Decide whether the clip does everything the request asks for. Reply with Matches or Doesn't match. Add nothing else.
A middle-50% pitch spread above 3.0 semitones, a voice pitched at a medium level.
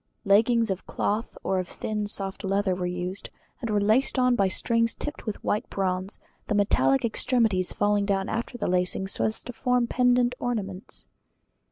Doesn't match